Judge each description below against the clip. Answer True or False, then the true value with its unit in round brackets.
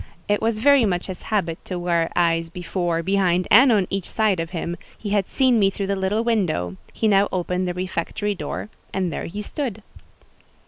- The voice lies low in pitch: False (190 Hz)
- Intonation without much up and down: False (3.2 semitones)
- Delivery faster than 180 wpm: True (190 wpm)